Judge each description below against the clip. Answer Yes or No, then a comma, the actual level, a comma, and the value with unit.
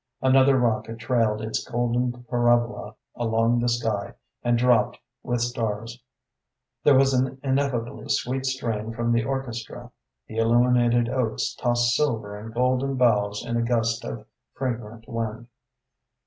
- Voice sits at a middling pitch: No, low, 120 Hz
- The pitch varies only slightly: Yes, narrow, 1.8 semitones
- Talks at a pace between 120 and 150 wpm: Yes, slow, 135 wpm